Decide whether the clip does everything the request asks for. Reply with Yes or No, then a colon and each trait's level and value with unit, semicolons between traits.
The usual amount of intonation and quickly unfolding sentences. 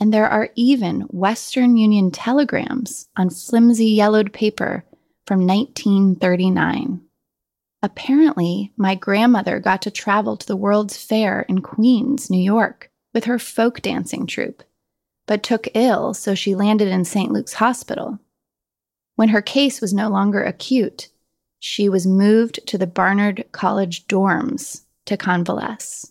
No: average, 3.3 semitones; slow, 135 wpm